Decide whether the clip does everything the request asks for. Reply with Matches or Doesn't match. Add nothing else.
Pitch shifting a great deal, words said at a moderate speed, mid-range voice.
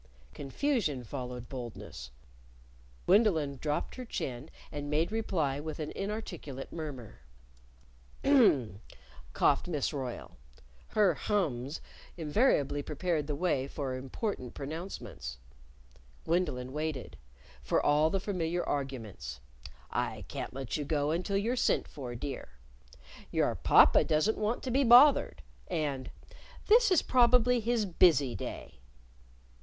Doesn't match